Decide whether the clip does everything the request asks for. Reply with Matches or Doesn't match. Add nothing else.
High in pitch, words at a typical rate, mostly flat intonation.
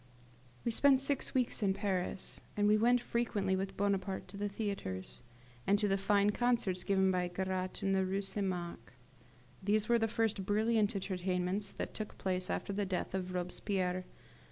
Matches